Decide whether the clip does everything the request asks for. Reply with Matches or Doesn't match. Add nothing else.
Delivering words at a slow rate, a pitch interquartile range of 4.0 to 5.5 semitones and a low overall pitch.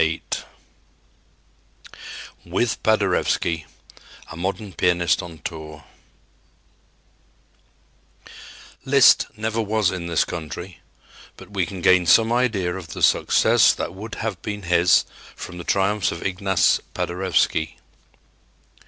Doesn't match